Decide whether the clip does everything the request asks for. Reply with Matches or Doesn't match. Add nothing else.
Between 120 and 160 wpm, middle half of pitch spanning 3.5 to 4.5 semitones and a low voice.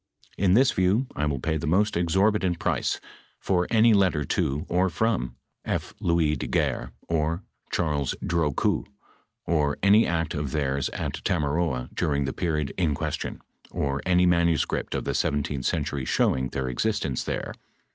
Matches